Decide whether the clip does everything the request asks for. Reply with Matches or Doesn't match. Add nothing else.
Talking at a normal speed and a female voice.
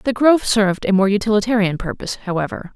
Matches